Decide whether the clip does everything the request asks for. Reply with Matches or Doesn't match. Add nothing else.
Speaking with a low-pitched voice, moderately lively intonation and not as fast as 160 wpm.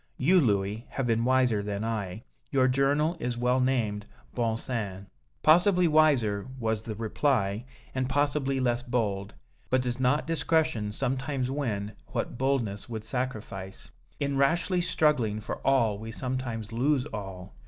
Matches